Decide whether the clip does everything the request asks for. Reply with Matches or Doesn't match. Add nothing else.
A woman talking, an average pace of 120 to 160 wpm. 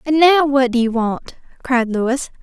Doesn't match